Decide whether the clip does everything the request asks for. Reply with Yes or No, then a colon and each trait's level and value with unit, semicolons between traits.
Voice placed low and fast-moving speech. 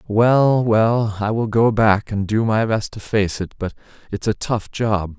Yes: low, 110 Hz; fast, 210 wpm